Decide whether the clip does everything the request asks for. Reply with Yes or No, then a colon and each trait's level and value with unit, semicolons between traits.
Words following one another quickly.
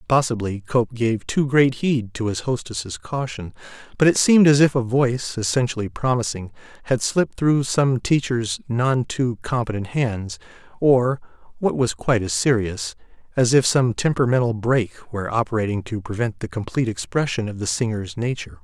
No: average, 155 wpm